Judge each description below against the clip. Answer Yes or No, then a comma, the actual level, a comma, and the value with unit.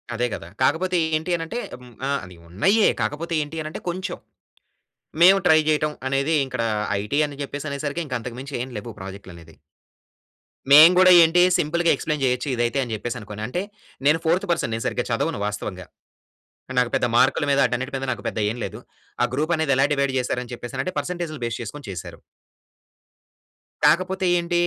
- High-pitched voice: No, medium, 140 Hz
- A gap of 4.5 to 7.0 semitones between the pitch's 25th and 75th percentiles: Yes, average, 5.1 semitones